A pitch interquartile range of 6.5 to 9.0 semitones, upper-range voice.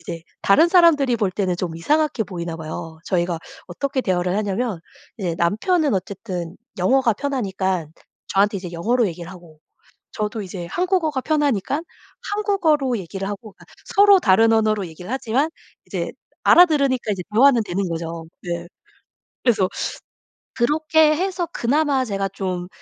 Yes: wide, 7.6 semitones; high, 210 Hz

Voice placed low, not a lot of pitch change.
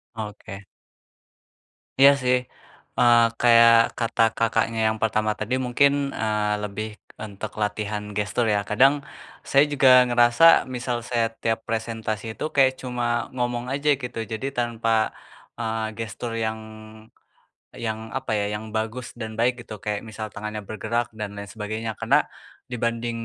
Yes: low, 115 Hz; narrow, 2.1 semitones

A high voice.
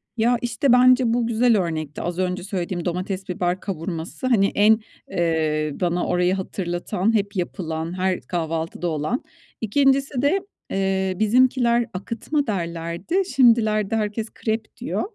Yes: high, 195 Hz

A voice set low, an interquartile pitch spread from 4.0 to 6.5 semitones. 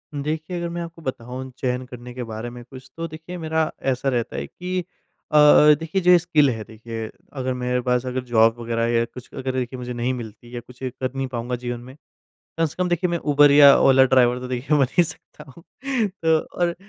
Yes: low, 130 Hz; average, 4.5 semitones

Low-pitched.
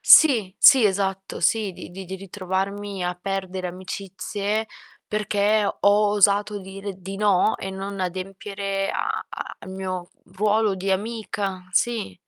No: high, 195 Hz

